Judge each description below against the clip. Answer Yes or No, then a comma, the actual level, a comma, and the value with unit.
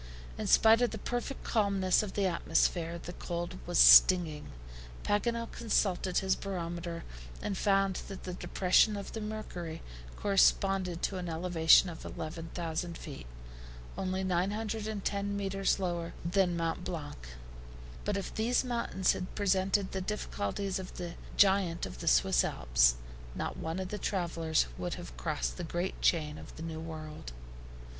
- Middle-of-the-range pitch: Yes, medium, 180 Hz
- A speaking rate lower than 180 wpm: Yes, average, 150 wpm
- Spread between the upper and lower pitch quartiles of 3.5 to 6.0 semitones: No, average, 3.1 semitones